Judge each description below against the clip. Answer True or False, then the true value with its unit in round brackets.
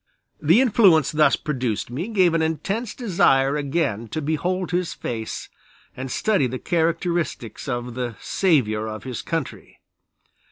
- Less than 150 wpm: True (135 wpm)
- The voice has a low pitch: False (155 Hz)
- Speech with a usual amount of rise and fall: False (6.0 semitones)